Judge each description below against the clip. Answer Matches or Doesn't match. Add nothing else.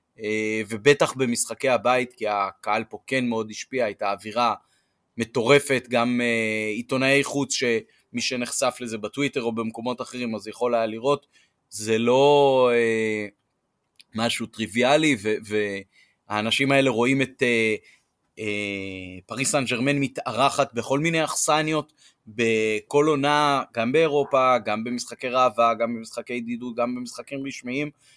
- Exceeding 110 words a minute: Matches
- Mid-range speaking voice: Doesn't match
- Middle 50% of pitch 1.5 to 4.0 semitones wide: Matches